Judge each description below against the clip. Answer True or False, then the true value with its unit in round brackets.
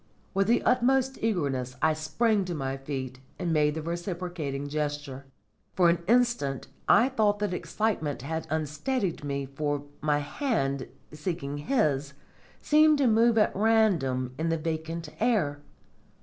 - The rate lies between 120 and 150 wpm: True (140 wpm)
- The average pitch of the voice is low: False (160 Hz)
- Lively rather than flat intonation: True (7.1 semitones)